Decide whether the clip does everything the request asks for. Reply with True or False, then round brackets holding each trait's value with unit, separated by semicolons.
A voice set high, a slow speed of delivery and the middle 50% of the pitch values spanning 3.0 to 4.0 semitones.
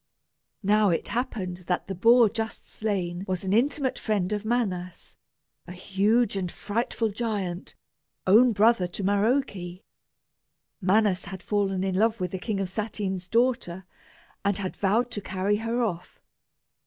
False (200 Hz; 145 wpm; 3.3 semitones)